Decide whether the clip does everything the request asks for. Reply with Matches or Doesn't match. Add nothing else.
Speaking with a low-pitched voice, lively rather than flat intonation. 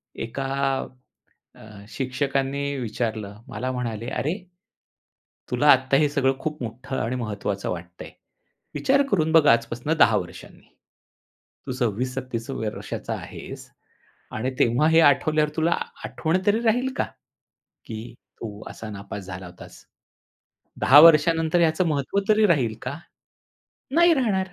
Matches